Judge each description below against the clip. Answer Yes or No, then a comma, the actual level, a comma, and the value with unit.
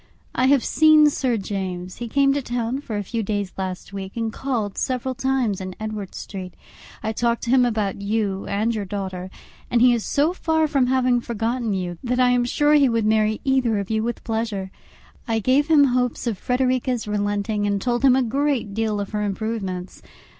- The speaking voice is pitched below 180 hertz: No, high, 225 Hz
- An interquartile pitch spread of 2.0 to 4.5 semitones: Yes, average, 3.9 semitones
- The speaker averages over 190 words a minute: Yes, average, 200 wpm